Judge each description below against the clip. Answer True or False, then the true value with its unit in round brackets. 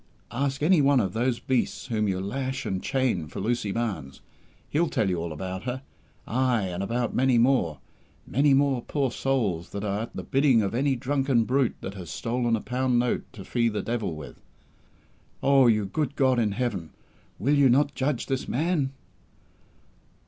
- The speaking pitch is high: False (120 Hz)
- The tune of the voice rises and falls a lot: False (4.8 semitones)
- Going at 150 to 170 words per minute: False (180 wpm)